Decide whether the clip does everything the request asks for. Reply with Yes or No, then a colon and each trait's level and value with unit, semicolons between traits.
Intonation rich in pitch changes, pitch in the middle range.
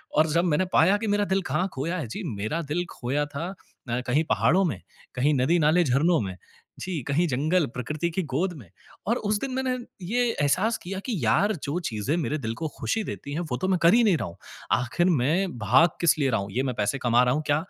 Yes: wide, 6.2 semitones; medium, 155 Hz